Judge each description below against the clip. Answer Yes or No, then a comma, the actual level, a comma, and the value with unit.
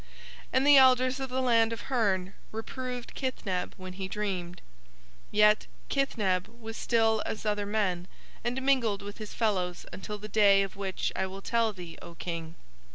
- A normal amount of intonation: Yes, average, 4.0 semitones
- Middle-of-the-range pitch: No, high, 210 Hz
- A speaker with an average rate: Yes, average, 165 wpm